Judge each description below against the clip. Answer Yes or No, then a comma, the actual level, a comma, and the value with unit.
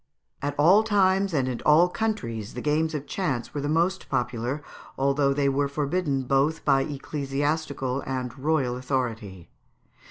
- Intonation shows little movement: No, average, 3.5 semitones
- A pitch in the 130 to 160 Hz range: Yes, medium, 140 Hz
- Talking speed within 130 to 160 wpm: Yes, average, 155 wpm